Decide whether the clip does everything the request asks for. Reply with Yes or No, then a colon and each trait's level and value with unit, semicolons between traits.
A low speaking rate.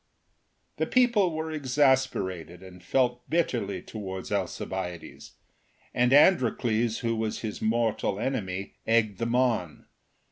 Yes: slow, 100 wpm